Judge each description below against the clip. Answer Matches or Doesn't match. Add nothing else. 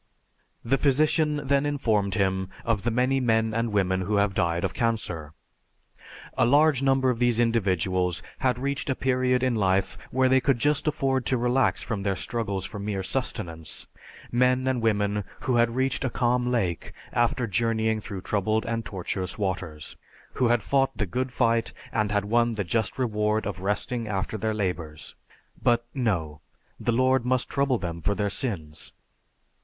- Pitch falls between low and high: Doesn't match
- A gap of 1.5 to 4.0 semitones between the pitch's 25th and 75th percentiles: Doesn't match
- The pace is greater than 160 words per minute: Matches